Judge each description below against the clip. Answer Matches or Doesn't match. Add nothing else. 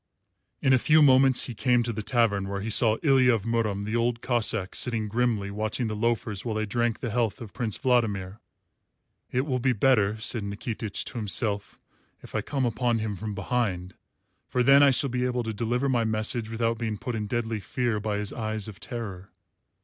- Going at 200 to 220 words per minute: Matches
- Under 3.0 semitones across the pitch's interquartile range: Matches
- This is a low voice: Matches